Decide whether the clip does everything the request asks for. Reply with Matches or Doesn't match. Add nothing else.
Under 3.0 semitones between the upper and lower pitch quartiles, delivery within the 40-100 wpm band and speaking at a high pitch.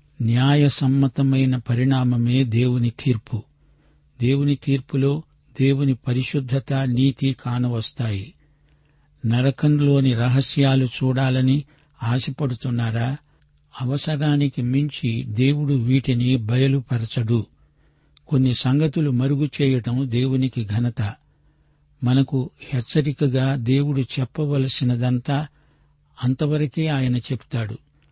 Doesn't match